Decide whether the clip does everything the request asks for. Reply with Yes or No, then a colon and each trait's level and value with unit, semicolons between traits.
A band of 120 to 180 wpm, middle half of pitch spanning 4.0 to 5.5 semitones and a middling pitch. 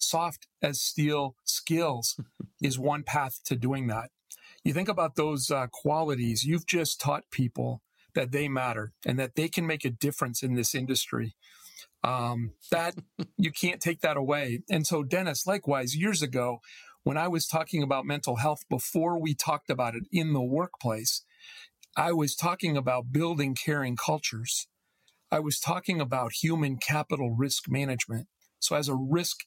Yes: average, 165 wpm; average, 4.3 semitones; medium, 145 Hz